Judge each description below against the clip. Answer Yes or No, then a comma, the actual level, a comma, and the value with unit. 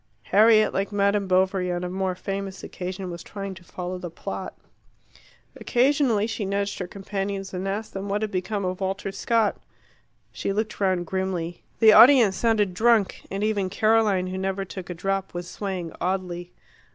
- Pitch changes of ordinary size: No, narrow, 2.1 semitones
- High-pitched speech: Yes, high, 195 Hz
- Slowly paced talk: No, average, 170 wpm